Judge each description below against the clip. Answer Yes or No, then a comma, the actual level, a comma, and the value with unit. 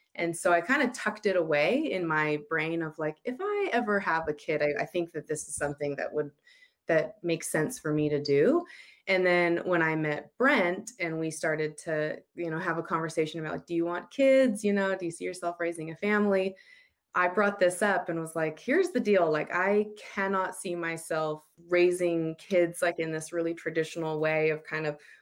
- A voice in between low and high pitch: Yes, medium, 170 Hz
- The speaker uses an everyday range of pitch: Yes, average, 3.4 semitones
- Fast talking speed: Yes, fast, 215 wpm